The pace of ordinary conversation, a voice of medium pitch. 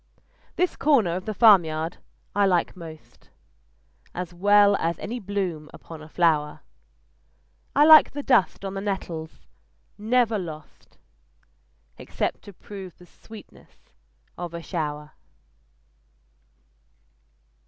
No: slow, 110 wpm; medium, 180 Hz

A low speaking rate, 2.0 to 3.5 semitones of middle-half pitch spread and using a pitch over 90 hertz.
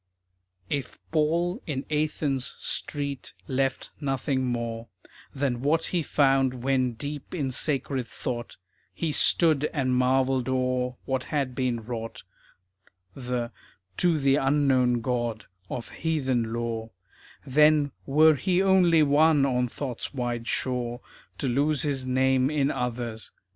Yes: slow, 125 wpm; average, 2.9 semitones; low, 135 Hz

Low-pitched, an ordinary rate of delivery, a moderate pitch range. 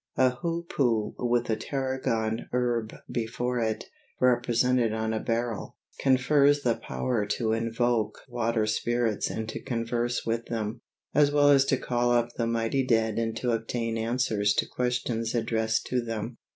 No: low, 120 Hz; average, 150 wpm; narrow, 1.8 semitones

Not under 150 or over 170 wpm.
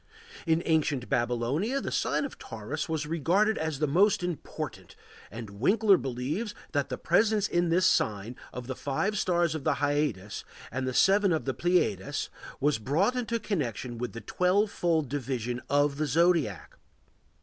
Yes: average, 160 wpm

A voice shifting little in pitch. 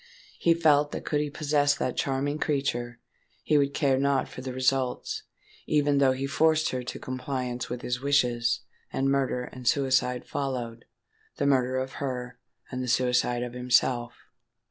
Yes: narrow, 2.2 semitones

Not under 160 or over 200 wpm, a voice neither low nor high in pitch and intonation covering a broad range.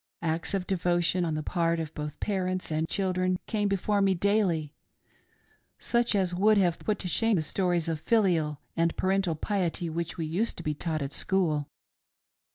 No: average, 175 wpm; medium, 175 Hz; average, 3.3 semitones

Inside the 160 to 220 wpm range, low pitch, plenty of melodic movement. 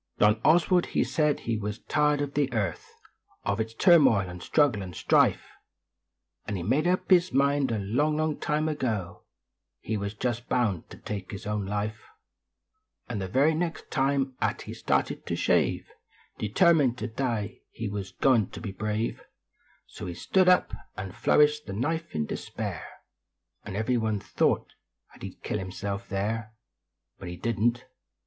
Yes: average, 170 wpm; low, 115 Hz; wide, 6.2 semitones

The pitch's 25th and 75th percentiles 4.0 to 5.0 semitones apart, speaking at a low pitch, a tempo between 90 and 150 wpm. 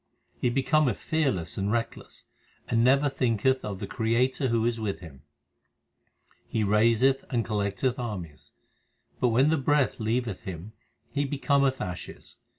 Yes: average, 4.3 semitones; low, 115 Hz; average, 140 wpm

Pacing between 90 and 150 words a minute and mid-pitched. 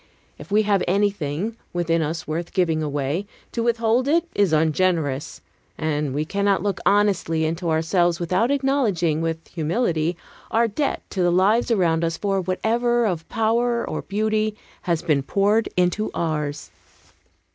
Yes: average, 145 wpm; medium, 180 Hz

